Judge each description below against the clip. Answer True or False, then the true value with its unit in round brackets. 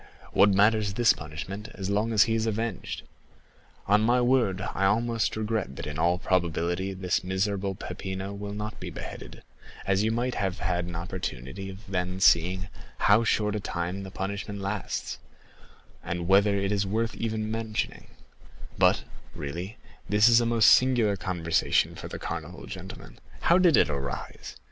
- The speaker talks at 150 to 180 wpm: True (165 wpm)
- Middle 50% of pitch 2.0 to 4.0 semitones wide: True (3.0 semitones)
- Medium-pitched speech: False (100 Hz)